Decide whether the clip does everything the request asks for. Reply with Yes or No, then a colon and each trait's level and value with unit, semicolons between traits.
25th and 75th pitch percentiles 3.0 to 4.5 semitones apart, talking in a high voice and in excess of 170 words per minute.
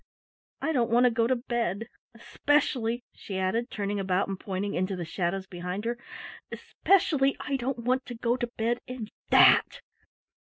No: average, 4.2 semitones; high, 230 Hz; average, 165 wpm